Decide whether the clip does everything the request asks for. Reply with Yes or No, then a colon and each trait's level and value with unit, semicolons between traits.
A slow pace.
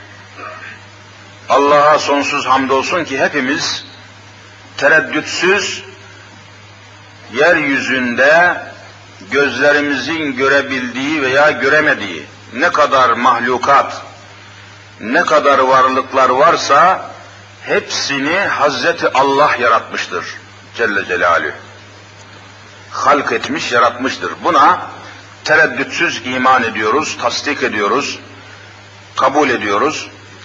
Yes: slow, 70 wpm